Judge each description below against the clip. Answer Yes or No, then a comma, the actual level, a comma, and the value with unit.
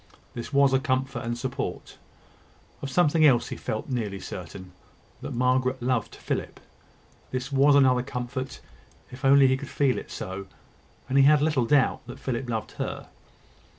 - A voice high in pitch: No, low, 130 Hz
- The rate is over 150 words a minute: Yes, average, 160 wpm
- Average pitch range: No, narrow, 2.3 semitones